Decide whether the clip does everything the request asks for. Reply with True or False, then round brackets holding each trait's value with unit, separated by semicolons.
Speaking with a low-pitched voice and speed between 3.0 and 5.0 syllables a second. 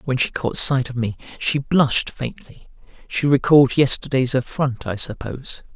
True (130 Hz; 4.8 syllables/s)